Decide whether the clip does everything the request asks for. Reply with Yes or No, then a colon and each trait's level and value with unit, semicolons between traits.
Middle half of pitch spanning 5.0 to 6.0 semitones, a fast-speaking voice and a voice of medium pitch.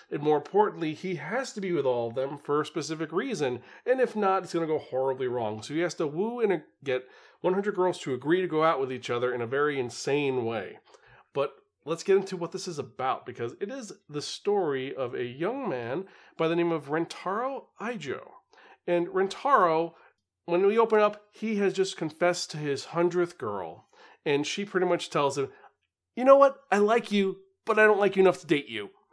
Yes: average, 5.3 semitones; fast, 215 wpm; medium, 175 Hz